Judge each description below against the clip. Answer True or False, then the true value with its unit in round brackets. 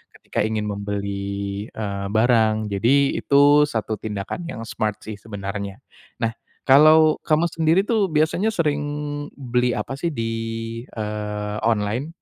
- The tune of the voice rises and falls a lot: True (6.1 semitones)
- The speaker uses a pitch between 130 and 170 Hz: False (110 Hz)